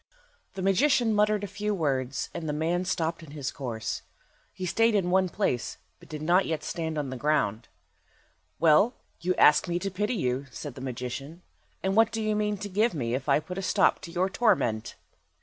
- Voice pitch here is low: No, medium, 175 Hz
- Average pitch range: No, wide, 6.1 semitones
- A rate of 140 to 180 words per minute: No, average, 200 wpm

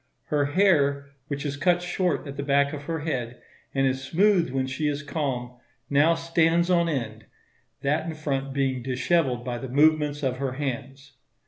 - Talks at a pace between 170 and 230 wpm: Yes, average, 180 wpm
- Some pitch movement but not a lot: Yes, average, 3.1 semitones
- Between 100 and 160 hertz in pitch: Yes, medium, 140 Hz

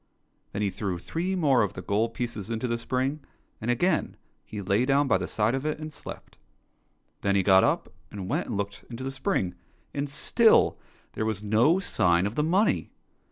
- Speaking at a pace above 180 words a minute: Yes, average, 200 wpm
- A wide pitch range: Yes, wide, 5.9 semitones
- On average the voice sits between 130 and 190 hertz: No, low, 115 Hz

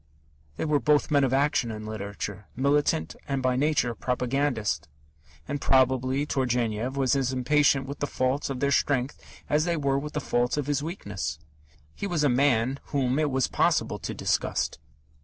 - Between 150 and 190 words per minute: Yes, average, 175 wpm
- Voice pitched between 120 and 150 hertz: Yes, low, 135 Hz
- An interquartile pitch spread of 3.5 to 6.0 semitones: No, average, 2.8 semitones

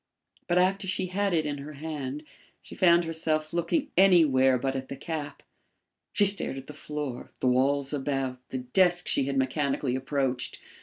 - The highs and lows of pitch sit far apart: No, average, 4.4 semitones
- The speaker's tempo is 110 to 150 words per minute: No, average, 170 wpm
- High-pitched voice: No, medium, 145 Hz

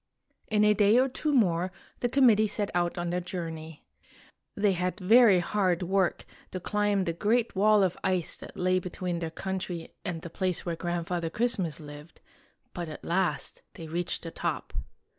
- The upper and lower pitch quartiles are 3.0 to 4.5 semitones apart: Yes, average, 3.3 semitones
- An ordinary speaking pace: Yes, average, 180 wpm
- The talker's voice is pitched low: No, medium, 185 Hz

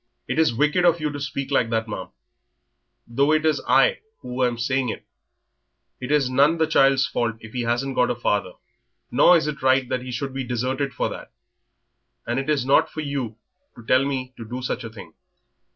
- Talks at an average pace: No, fast, 215 wpm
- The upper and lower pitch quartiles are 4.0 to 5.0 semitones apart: No, average, 3.1 semitones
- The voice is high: No, low, 130 Hz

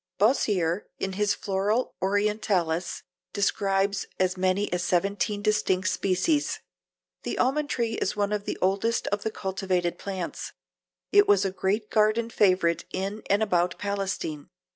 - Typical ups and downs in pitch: No, narrow, 2.2 semitones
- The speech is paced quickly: No, average, 140 wpm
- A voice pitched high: Yes, high, 200 Hz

